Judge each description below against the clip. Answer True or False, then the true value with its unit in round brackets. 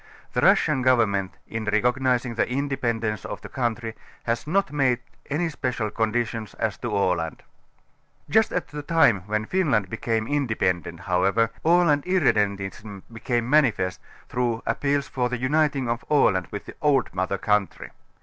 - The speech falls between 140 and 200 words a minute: True (150 wpm)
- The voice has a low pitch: True (120 Hz)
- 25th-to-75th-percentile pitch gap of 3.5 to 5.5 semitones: True (4.9 semitones)